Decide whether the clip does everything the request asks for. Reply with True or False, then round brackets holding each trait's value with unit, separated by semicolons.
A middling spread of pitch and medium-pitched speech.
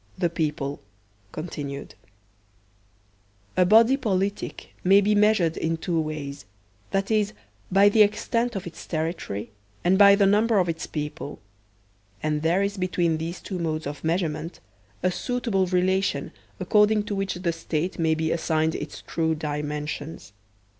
True (4.2 semitones; 175 Hz)